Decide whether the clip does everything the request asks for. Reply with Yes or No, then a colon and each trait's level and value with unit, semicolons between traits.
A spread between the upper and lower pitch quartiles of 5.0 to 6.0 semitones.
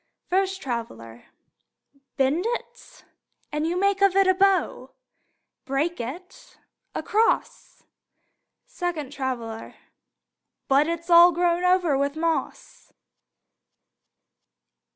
Yes: wide, 5.4 semitones